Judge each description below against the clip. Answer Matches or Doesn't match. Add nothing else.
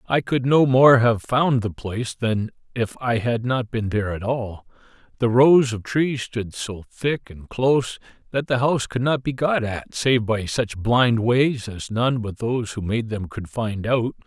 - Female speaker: Doesn't match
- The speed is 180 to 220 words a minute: Matches